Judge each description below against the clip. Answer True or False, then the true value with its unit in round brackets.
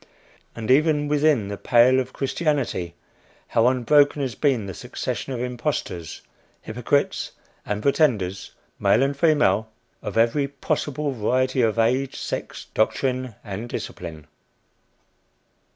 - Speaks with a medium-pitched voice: False (125 Hz)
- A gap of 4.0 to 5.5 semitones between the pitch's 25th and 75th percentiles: True (4.3 semitones)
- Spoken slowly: True (120 wpm)